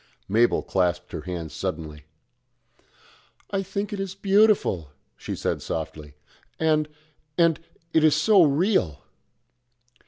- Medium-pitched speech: Yes, medium, 150 Hz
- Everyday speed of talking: No, slow, 115 wpm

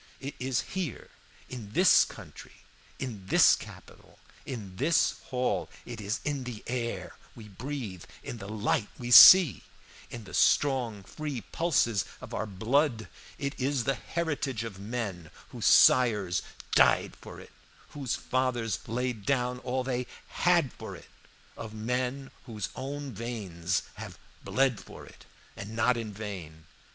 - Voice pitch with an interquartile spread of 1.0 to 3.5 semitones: No, average, 4.1 semitones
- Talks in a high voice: No, low, 120 Hz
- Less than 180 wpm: Yes, average, 145 wpm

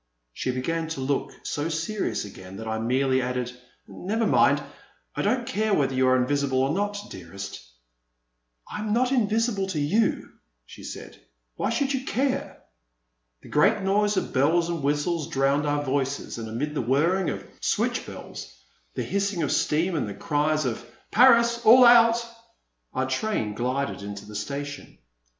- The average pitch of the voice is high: No, medium, 150 Hz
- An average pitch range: No, wide, 8.0 semitones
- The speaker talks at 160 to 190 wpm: Yes, average, 170 wpm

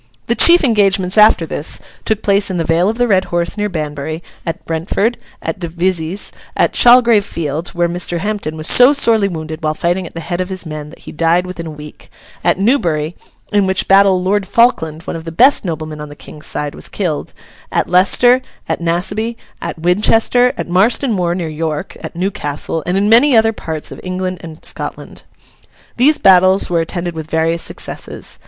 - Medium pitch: Yes, medium, 180 Hz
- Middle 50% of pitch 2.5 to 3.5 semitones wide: No, average, 4.2 semitones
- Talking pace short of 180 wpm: No, average, 190 wpm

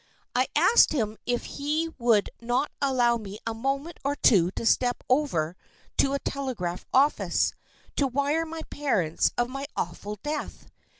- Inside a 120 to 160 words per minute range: Yes, average, 155 wpm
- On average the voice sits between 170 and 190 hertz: No, very high, 255 Hz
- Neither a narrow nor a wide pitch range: Yes, average, 4.4 semitones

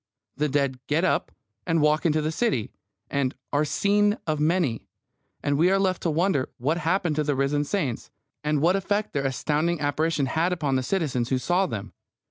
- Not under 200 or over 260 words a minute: No, average, 190 wpm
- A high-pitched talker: No, medium, 155 Hz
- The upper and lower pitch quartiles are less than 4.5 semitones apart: Yes, average, 4.0 semitones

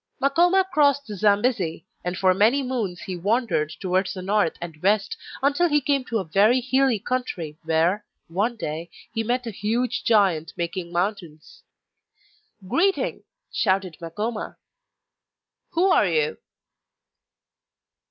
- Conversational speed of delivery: No, slow, 130 wpm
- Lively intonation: Yes, wide, 6.2 semitones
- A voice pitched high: Yes, high, 210 Hz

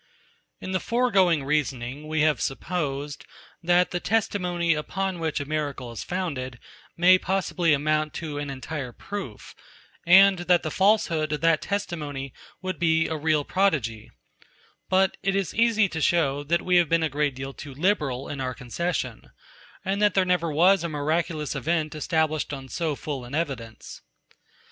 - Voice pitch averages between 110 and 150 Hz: No, medium, 160 Hz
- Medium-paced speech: Yes, average, 165 wpm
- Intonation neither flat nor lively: Yes, average, 4.0 semitones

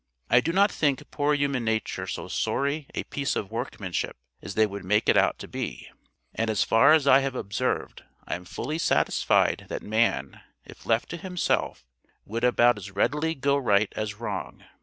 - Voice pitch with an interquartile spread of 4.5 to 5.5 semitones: Yes, average, 5.1 semitones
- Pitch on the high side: No, low, 125 Hz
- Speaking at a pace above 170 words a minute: Yes, average, 185 wpm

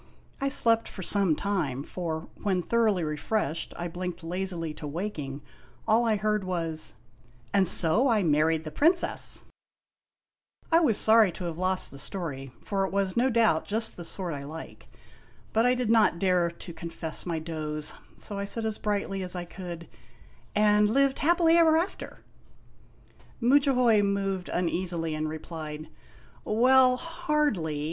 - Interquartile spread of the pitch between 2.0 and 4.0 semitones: No, wide, 5.5 semitones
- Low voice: No, high, 190 Hz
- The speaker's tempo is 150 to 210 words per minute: Yes, average, 160 wpm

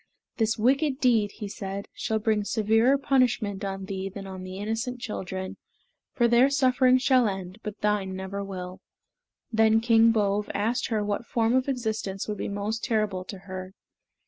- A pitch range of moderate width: Yes, average, 3.3 semitones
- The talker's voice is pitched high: Yes, high, 215 Hz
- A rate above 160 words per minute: Yes, average, 170 wpm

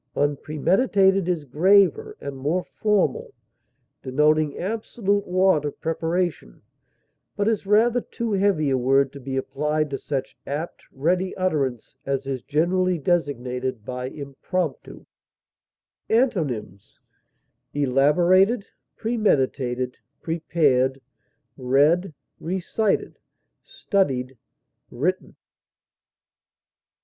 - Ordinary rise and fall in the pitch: No, wide, 5.8 semitones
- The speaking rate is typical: No, slow, 90 wpm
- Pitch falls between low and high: Yes, medium, 155 Hz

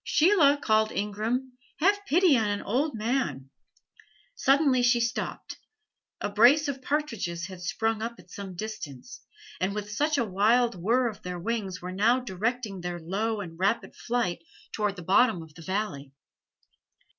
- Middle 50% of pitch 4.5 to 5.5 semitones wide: Yes, average, 5.0 semitones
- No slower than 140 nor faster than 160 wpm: Yes, average, 155 wpm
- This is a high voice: Yes, high, 215 Hz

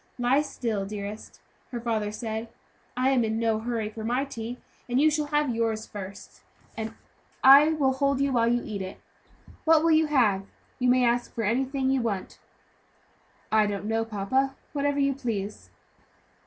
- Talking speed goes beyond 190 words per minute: No, average, 170 wpm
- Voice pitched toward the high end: Yes, high, 240 Hz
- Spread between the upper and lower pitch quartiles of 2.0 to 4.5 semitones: Yes, average, 3.8 semitones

